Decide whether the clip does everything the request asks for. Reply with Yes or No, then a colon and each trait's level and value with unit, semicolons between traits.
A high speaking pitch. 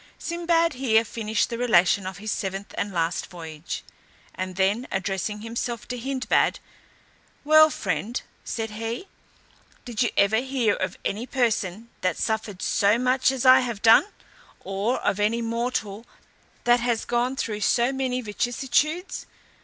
Yes: high, 230 Hz